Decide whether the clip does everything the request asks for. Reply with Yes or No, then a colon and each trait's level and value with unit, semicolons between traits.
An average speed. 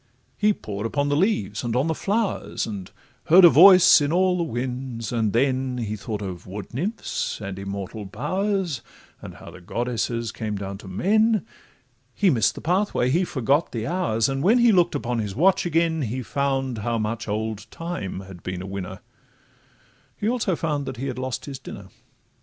Yes: average, 185 wpm